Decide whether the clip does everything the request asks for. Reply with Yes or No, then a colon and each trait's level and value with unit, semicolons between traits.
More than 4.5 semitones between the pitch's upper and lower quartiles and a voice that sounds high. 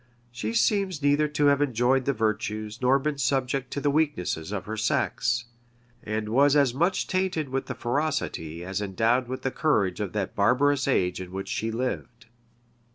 No: average, 4.9 semitones; low, 125 Hz